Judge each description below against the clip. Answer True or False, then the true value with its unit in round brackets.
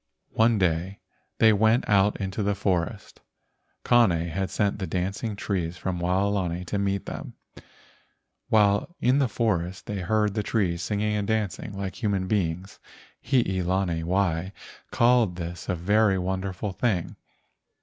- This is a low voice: True (100 Hz)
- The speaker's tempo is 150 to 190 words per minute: False (140 wpm)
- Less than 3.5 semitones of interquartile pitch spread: True (2.7 semitones)